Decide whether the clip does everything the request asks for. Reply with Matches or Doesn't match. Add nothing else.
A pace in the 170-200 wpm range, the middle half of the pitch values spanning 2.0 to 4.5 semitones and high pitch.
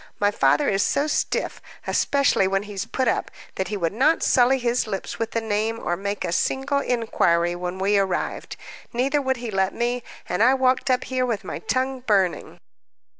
Doesn't match